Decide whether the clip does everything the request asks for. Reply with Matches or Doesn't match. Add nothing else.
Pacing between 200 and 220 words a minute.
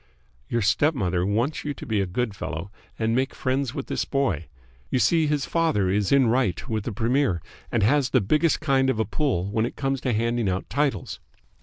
Matches